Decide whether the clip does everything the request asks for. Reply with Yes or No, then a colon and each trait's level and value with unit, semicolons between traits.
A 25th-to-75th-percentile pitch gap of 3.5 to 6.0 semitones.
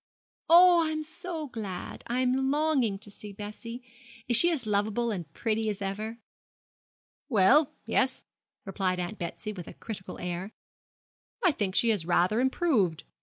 Yes: average, 5.3 semitones